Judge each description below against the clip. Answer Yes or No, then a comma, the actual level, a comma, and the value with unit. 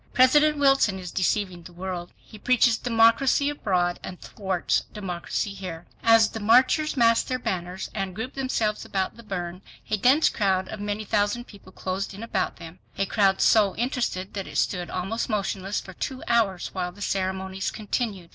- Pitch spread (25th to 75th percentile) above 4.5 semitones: No, average, 3.6 semitones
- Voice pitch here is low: No, high, 200 Hz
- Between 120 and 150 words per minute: No, average, 175 wpm